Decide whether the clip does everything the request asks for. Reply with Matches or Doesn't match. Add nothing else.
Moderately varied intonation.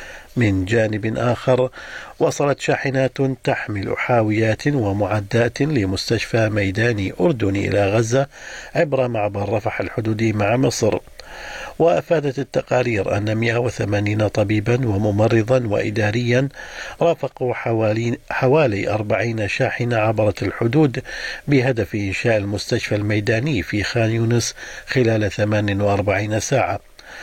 Matches